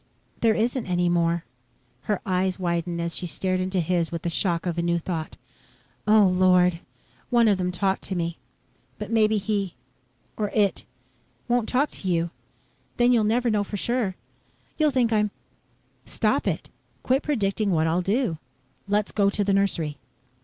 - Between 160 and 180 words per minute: Yes, average, 170 wpm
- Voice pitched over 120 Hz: Yes, high, 190 Hz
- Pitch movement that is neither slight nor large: Yes, average, 3.8 semitones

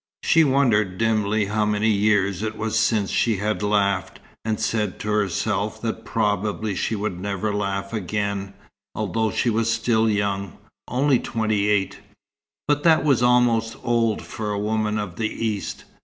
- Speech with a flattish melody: Yes, narrow, 1.8 semitones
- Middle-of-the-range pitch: No, low, 105 Hz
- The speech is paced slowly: No, average, 155 wpm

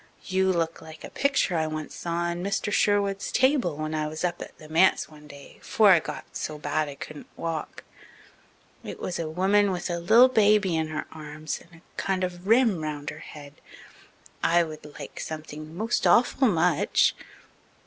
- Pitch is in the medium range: Yes, medium, 170 Hz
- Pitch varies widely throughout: No, average, 3.9 semitones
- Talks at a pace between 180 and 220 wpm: Yes, average, 185 wpm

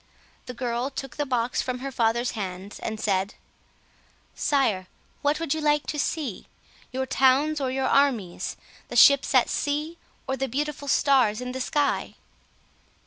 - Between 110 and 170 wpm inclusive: Yes, average, 155 wpm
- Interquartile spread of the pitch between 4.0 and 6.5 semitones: No, average, 3.4 semitones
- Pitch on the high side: Yes, very high, 265 Hz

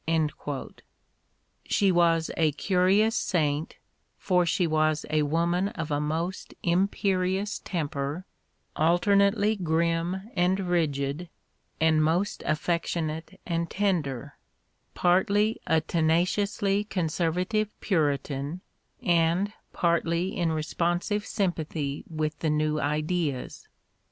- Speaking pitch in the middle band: Yes, medium, 170 Hz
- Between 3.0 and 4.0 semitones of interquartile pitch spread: Yes, average, 3.4 semitones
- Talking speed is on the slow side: Yes, slow, 95 wpm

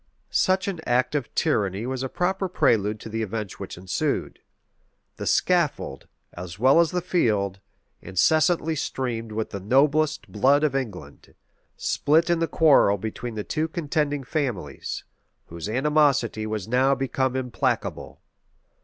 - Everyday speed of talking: Yes, average, 145 wpm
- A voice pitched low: Yes, low, 130 Hz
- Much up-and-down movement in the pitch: Yes, wide, 6.3 semitones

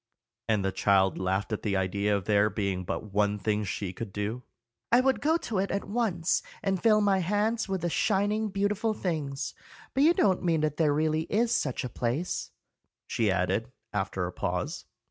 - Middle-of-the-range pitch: Yes, medium, 150 Hz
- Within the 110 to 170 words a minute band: No, average, 190 wpm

